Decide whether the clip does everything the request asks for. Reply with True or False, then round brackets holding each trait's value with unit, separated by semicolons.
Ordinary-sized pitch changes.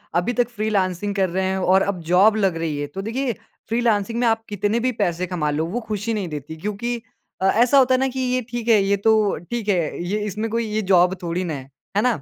True (4.1 semitones)